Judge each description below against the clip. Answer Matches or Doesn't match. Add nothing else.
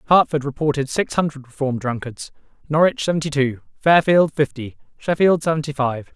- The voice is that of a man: Matches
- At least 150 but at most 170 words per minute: Doesn't match